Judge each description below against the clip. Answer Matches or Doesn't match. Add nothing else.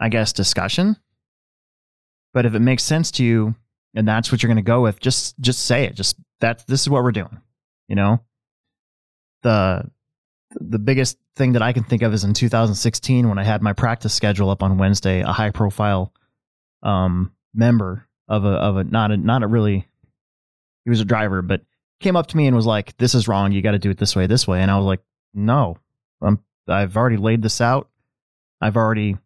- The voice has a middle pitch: Doesn't match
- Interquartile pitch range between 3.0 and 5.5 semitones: Matches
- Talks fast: Matches